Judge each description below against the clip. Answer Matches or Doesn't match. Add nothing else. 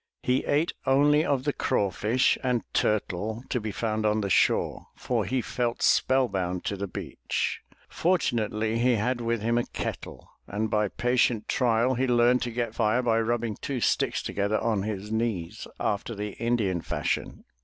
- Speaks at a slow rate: Doesn't match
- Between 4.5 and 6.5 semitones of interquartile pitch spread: Doesn't match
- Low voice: Matches